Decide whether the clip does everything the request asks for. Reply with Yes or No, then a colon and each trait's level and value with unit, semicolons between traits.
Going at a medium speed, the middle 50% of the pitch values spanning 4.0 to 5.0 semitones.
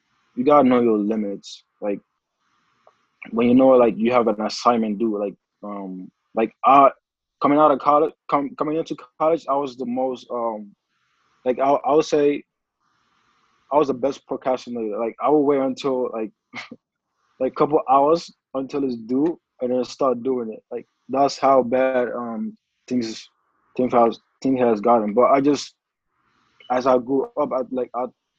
No: average, 170 wpm; average, 3.0 semitones